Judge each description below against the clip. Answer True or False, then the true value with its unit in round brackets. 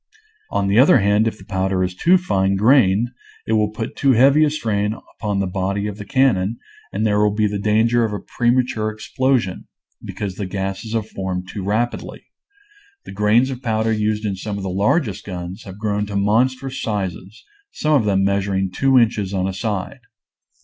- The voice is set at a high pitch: False (105 Hz)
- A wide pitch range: False (3.1 semitones)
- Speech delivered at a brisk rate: False (195 wpm)